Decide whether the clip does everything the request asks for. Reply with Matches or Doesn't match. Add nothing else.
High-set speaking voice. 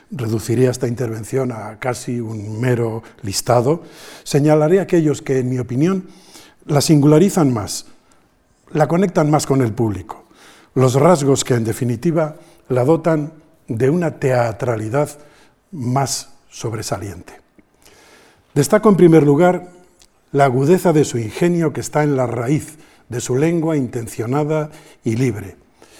Doesn't match